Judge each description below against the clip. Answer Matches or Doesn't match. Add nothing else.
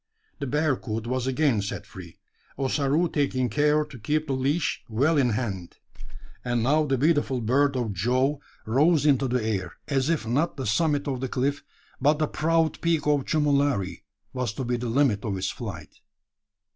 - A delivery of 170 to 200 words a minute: Matches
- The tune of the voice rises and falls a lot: Doesn't match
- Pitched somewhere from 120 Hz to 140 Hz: Matches